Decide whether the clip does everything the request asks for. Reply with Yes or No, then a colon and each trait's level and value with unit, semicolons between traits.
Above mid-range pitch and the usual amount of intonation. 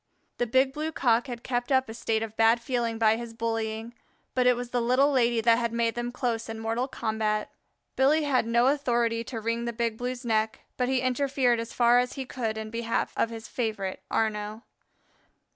No: high, 235 Hz; narrow, 1.8 semitones